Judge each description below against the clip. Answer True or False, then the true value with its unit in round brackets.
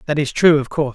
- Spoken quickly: True (315 wpm)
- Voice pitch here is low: False (145 Hz)